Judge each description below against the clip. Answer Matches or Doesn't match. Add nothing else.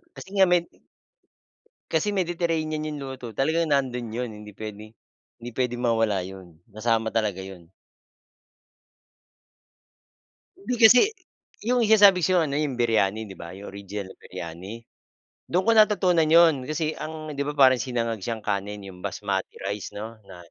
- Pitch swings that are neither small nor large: Doesn't match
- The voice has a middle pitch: Doesn't match